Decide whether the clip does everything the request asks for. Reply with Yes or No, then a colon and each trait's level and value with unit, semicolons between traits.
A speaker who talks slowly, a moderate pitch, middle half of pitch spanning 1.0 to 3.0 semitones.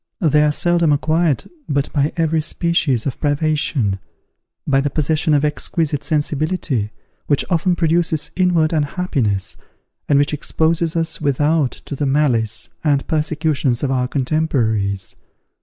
Yes: slow, 130 wpm; medium, 150 Hz; average, 2.7 semitones